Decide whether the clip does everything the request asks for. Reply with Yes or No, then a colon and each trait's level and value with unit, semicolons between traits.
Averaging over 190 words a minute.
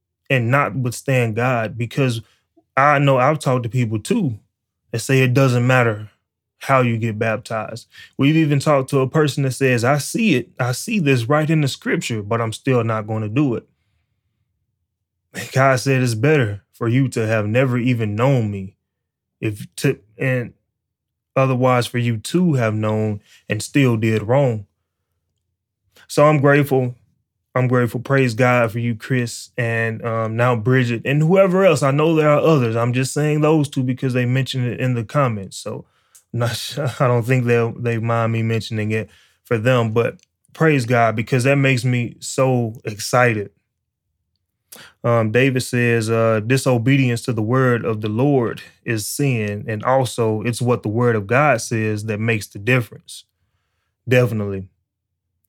No: average, 170 wpm